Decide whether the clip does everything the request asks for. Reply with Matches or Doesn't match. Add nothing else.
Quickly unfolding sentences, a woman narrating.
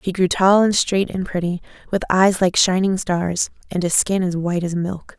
Matches